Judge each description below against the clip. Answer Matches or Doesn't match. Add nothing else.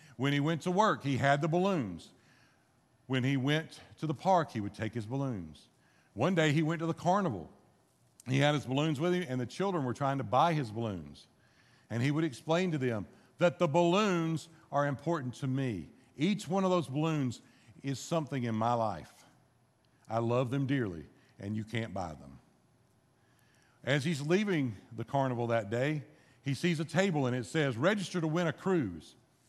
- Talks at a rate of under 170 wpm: Doesn't match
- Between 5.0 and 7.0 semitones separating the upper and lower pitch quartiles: Matches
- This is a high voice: Doesn't match